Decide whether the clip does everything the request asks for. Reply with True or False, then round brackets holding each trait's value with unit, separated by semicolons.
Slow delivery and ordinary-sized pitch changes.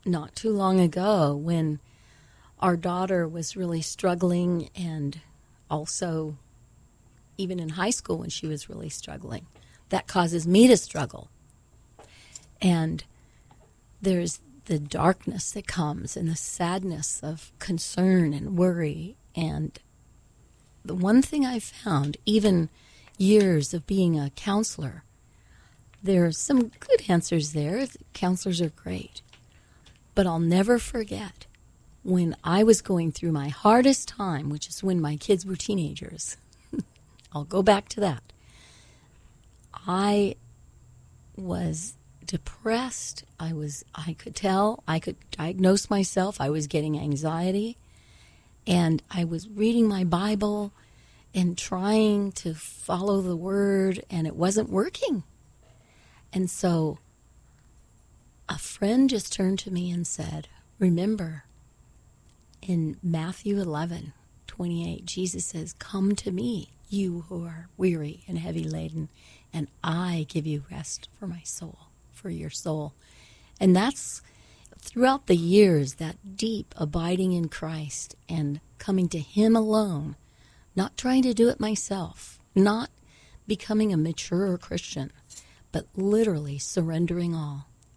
True (125 wpm; 4.2 semitones)